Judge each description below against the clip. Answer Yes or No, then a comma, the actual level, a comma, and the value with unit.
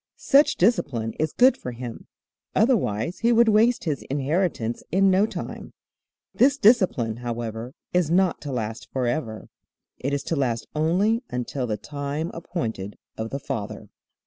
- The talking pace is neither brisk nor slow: Yes, average, 145 wpm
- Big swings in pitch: Yes, wide, 8.3 semitones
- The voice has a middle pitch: Yes, medium, 145 Hz